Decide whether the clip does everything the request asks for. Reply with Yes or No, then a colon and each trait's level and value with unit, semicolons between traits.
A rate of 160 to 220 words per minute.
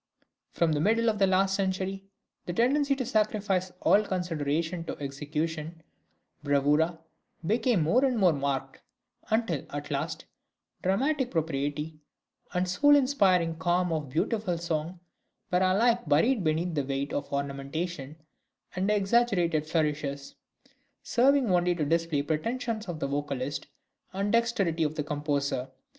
No: average, 140 wpm